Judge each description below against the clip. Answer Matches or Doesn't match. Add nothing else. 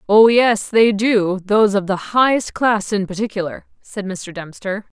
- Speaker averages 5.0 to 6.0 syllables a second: Doesn't match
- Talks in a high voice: Matches